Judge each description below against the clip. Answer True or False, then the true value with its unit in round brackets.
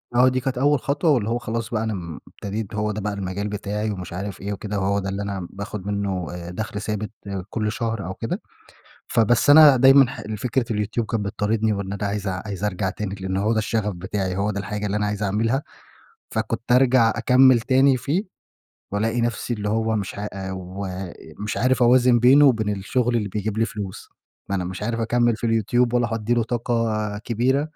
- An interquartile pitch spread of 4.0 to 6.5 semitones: False (3.0 semitones)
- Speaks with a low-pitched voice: True (105 Hz)